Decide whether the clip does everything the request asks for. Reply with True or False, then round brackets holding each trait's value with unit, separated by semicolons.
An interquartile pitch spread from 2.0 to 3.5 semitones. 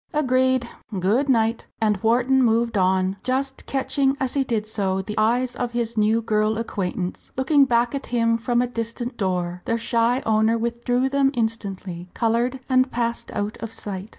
True (3.0 semitones)